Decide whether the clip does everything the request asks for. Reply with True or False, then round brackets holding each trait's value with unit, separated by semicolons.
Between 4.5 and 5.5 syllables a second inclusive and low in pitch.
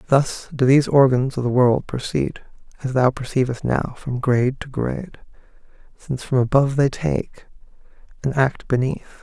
True (5.0 syllables/s; 130 Hz)